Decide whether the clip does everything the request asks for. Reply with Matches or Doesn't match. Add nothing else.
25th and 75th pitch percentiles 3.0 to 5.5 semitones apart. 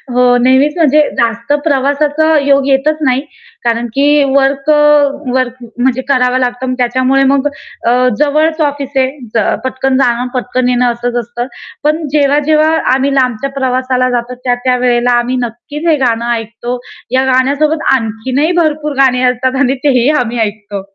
Doesn't match